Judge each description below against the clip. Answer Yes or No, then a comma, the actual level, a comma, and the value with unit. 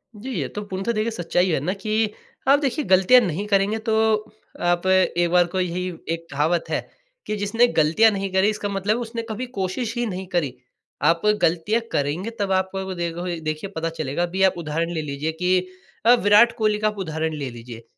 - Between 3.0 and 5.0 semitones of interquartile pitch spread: Yes, average, 4.2 semitones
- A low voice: No, medium, 185 Hz